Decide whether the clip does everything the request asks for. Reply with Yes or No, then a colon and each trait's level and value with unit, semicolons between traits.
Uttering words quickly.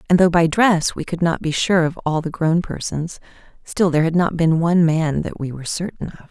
Yes: fast, 245 wpm